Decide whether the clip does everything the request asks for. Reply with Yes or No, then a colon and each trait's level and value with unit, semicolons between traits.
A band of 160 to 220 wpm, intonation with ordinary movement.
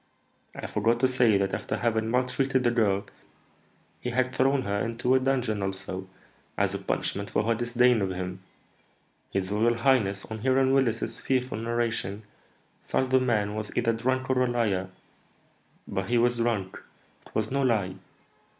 Yes: average, 165 wpm; average, 3.8 semitones